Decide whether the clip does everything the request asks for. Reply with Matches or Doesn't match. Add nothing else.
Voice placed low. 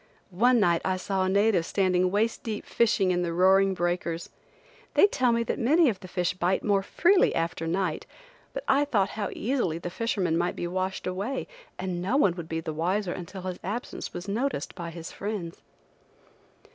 Doesn't match